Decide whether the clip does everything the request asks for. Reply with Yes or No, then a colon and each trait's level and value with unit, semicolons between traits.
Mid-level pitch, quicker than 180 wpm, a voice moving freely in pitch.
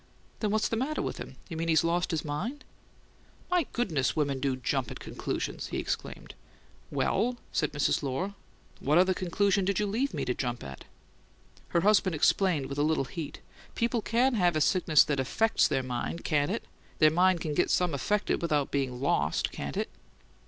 Yes: medium, 165 Hz; average, 190 wpm; wide, 6.1 semitones